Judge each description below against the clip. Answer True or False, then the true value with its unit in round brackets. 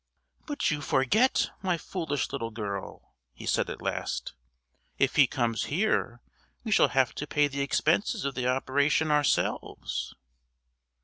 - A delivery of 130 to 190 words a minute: True (140 wpm)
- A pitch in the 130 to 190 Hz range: True (140 Hz)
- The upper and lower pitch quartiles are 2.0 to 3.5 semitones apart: False (4.1 semitones)